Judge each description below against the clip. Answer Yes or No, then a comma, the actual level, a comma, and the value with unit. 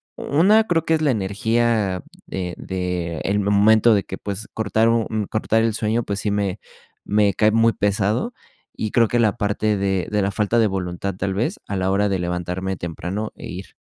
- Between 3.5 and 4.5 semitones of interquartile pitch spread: No, average, 2.8 semitones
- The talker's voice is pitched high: No, low, 105 Hz